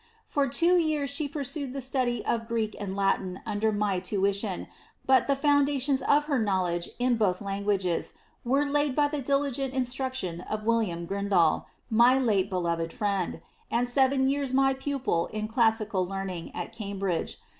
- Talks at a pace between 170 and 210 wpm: No, average, 155 wpm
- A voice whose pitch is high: Yes, high, 230 Hz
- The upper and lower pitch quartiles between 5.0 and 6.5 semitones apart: Yes, wide, 5.6 semitones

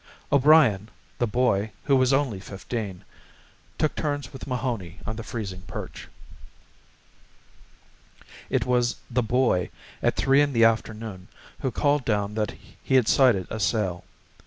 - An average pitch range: Yes, average, 4.3 semitones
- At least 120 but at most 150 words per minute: Yes, slow, 135 wpm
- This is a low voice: Yes, low, 115 Hz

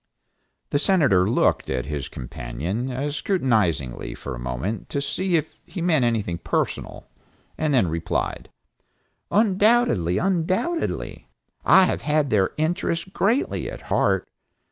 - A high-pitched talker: No, medium, 140 Hz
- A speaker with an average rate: No, slow, 120 wpm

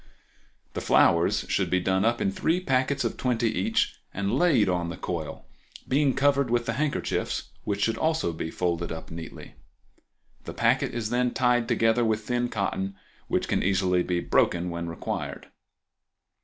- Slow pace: No, average, 160 wpm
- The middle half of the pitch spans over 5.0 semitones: Yes, wide, 5.4 semitones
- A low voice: Yes, low, 110 Hz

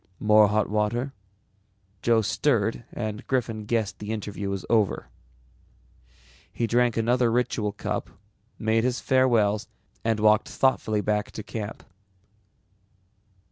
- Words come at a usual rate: No, slow, 115 wpm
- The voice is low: Yes, low, 110 Hz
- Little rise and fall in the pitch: Yes, narrow, 2.1 semitones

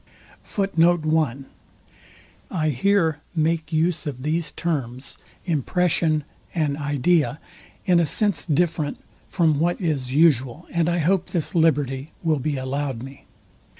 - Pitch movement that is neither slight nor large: Yes, average, 3.2 semitones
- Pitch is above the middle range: No, medium, 155 Hz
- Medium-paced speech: No, slow, 115 wpm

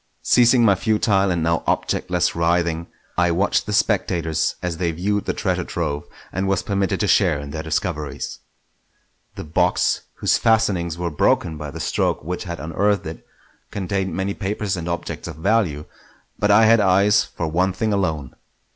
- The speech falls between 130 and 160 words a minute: No, average, 170 wpm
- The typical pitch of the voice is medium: No, very low, 90 Hz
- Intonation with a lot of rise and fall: No, average, 3.5 semitones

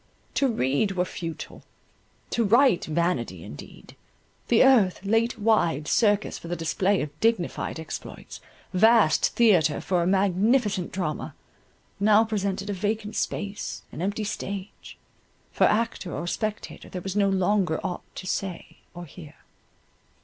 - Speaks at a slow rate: Yes, slow, 130 wpm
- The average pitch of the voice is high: Yes, high, 195 Hz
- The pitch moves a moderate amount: Yes, average, 3.6 semitones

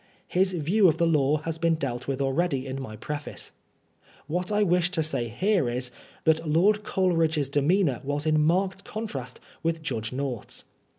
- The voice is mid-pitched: Yes, medium, 155 Hz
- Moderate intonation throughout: Yes, average, 4.7 semitones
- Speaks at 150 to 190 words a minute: Yes, average, 170 wpm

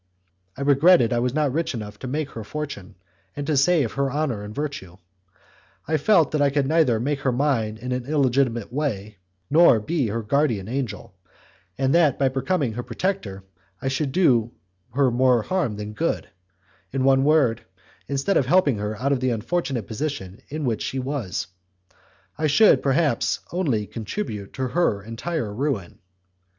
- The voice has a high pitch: No, low, 135 Hz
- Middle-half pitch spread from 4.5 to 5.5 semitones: Yes, average, 4.9 semitones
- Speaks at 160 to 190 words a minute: Yes, average, 170 wpm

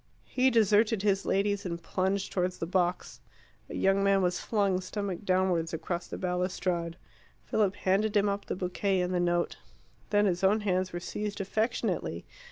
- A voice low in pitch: No, high, 190 Hz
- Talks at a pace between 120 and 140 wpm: No, average, 170 wpm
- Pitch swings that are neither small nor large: No, narrow, 2.2 semitones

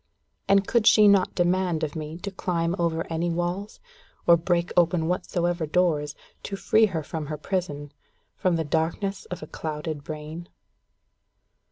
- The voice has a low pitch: No, medium, 170 Hz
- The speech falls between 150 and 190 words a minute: Yes, average, 155 wpm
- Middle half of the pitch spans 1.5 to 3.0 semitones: Yes, narrow, 2.6 semitones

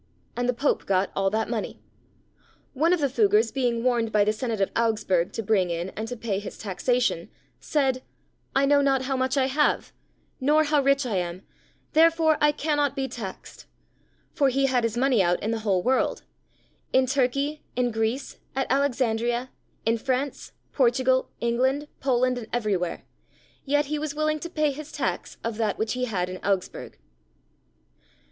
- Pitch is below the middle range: No, very high, 250 Hz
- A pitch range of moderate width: Yes, average, 4.1 semitones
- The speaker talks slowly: No, average, 170 wpm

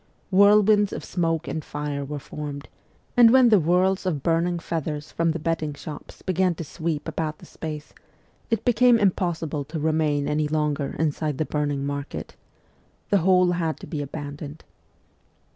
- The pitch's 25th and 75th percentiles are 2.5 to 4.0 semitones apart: Yes, average, 3.5 semitones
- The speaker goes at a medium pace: Yes, average, 160 wpm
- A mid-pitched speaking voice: Yes, medium, 160 Hz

